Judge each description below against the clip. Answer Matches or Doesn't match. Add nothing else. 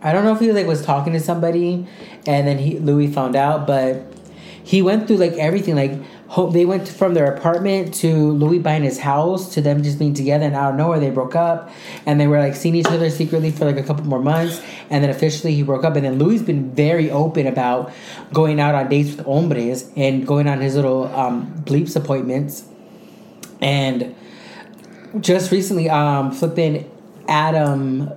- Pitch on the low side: Doesn't match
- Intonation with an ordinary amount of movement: Matches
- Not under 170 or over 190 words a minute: Doesn't match